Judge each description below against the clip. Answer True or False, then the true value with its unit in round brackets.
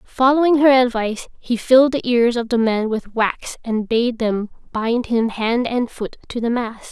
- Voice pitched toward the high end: True (235 Hz)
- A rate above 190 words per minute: True (200 wpm)